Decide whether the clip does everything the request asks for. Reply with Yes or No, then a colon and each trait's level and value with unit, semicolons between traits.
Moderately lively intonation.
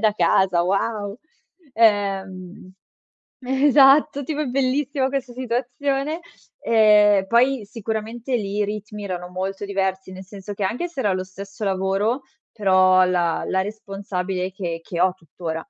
Yes: average, 4.4 semitones